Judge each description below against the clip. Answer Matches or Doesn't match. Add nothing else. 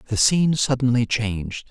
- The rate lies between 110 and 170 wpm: Matches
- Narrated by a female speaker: Doesn't match